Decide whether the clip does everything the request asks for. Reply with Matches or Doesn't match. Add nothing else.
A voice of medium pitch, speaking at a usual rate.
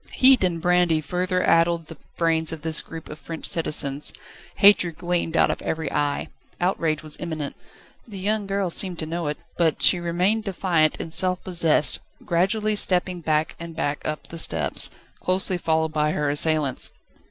Matches